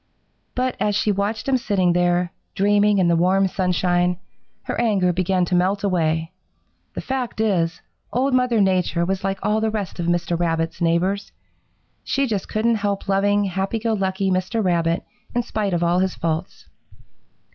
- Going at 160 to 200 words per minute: Yes, average, 170 wpm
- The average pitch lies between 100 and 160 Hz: No, high, 190 Hz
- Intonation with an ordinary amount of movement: Yes, average, 3.0 semitones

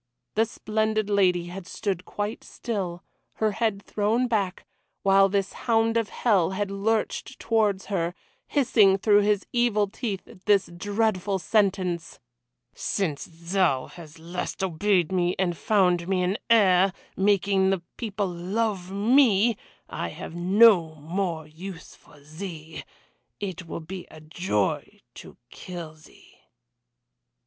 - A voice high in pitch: Yes, high, 195 Hz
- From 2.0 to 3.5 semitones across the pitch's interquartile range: Yes, average, 3.1 semitones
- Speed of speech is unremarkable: No, slow, 130 wpm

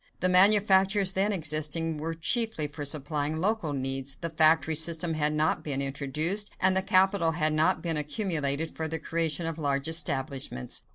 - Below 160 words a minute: No, average, 165 wpm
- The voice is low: No, medium, 160 Hz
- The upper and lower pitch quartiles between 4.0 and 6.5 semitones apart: No, average, 3.6 semitones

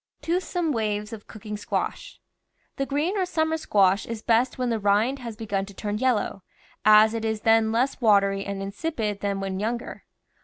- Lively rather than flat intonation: No, average, 3.7 semitones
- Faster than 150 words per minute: Yes, average, 180 wpm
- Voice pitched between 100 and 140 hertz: No, high, 220 Hz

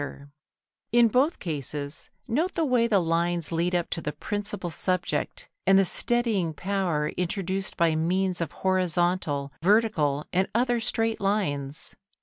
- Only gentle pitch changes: No, average, 4.7 semitones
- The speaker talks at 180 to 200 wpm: No, average, 145 wpm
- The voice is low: No, medium, 185 Hz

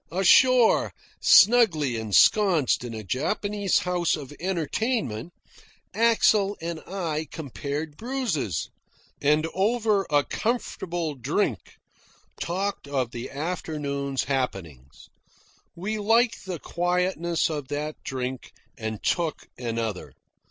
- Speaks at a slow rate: Yes, slow, 100 wpm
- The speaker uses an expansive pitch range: Yes, wide, 6.7 semitones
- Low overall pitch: No, medium, 160 Hz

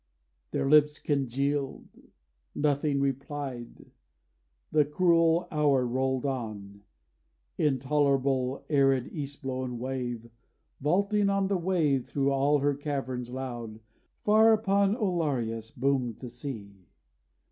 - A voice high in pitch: No, medium, 140 Hz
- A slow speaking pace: Yes, slow, 100 wpm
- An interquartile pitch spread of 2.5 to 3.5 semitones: Yes, average, 3.1 semitones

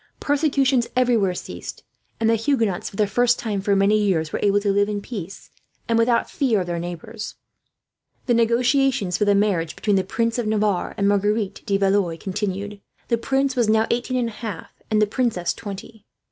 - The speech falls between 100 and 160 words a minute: No, average, 190 wpm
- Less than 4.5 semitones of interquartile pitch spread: Yes, average, 3.0 semitones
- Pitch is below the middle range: No, high, 210 Hz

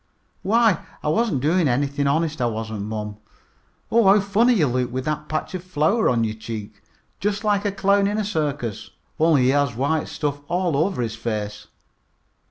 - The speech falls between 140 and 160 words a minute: No, average, 180 wpm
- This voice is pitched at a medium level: Yes, medium, 150 Hz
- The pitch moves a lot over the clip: Yes, wide, 8.1 semitones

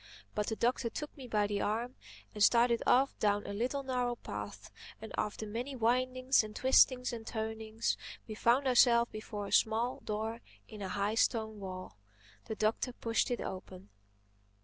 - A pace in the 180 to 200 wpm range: No, average, 170 wpm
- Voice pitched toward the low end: No, high, 225 Hz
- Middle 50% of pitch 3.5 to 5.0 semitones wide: No, average, 2.7 semitones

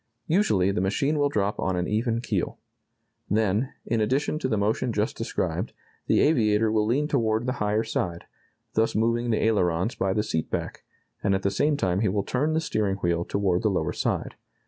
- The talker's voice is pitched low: Yes, low, 110 Hz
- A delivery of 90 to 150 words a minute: No, average, 195 wpm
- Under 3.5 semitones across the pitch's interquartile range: No, average, 3.8 semitones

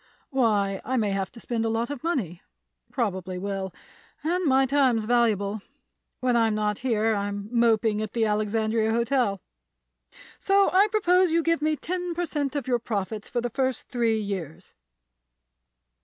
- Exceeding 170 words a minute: No, average, 160 wpm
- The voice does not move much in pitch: No, average, 4.4 semitones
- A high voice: Yes, high, 230 Hz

